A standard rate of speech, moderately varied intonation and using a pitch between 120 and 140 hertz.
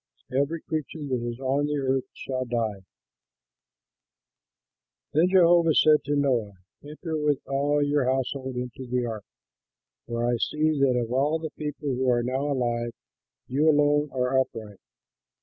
Yes: average, 150 wpm; average, 3.1 semitones; low, 135 Hz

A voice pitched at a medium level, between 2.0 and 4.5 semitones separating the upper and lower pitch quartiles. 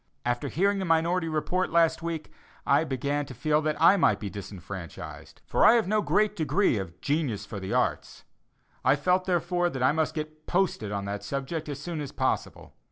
No: medium, 155 Hz; average, 5.3 semitones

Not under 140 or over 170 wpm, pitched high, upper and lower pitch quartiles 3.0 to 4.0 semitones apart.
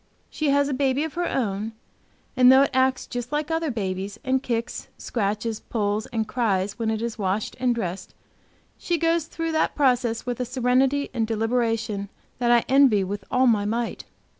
No: average, 185 wpm; high, 240 Hz; average, 3.6 semitones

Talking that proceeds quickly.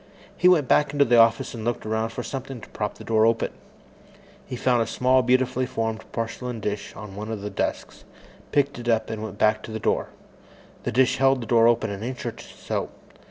Yes: fast, 215 wpm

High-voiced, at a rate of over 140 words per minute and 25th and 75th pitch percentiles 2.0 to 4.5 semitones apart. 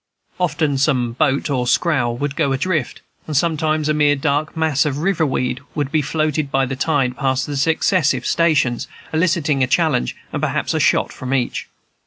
No: medium, 145 Hz; average, 180 wpm; average, 2.9 semitones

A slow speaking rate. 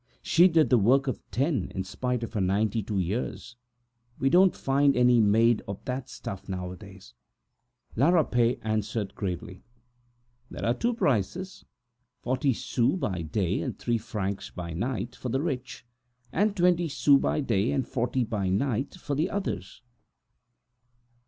No: average, 150 wpm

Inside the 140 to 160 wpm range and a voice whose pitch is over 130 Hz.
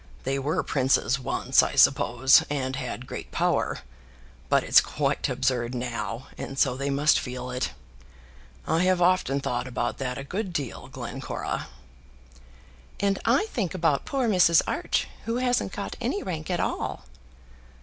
Yes: average, 150 wpm; medium, 140 Hz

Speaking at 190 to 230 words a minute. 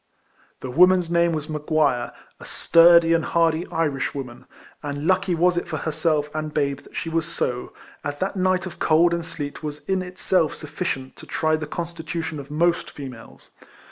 No: average, 170 wpm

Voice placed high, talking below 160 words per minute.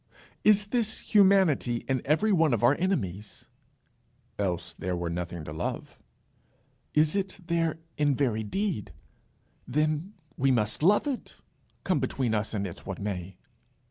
No: low, 135 Hz; average, 140 wpm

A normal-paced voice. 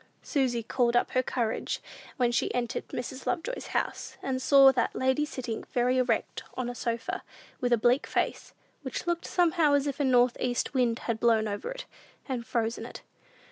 Yes: average, 185 wpm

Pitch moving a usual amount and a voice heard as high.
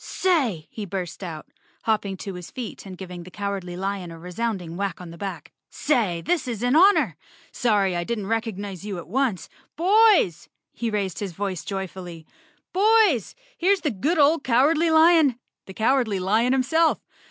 No: wide, 6.9 semitones; high, 210 Hz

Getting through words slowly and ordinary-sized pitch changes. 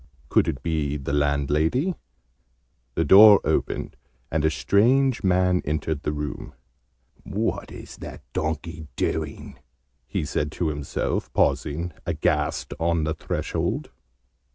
Yes: slow, 120 wpm; average, 3.5 semitones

